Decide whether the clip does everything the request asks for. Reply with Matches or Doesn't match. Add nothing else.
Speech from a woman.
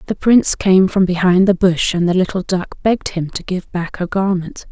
Matches